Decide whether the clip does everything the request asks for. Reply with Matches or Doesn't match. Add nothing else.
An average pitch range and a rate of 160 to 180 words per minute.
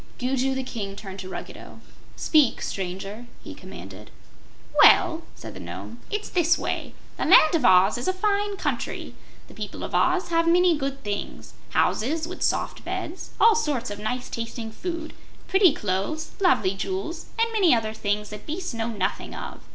Doesn't match